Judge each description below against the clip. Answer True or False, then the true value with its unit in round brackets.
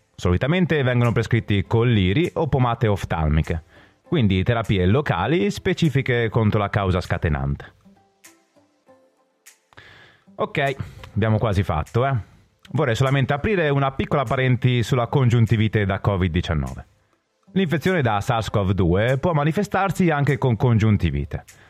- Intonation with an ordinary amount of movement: False (6.1 semitones)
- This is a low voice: True (115 Hz)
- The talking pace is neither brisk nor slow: False (105 wpm)